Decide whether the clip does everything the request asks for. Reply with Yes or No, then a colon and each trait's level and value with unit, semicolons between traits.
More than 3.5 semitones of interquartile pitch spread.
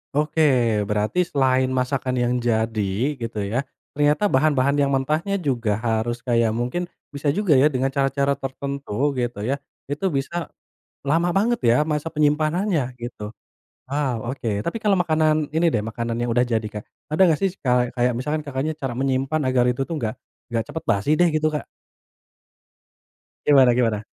Yes: average, 4.2 semitones